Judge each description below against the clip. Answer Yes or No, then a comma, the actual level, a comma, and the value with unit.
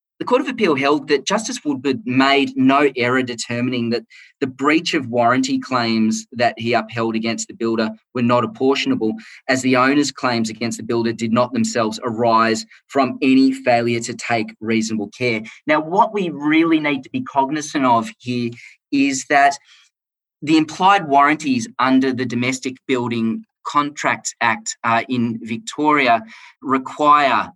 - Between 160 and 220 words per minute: No, average, 150 wpm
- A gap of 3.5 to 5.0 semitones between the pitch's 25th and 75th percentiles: Yes, average, 3.9 semitones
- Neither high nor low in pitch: No, low, 130 Hz